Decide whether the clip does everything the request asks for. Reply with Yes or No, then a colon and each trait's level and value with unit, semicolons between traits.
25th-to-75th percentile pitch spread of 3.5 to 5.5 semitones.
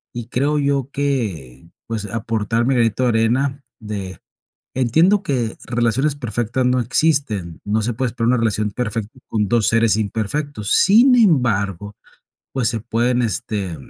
Yes: average, 3.8 semitones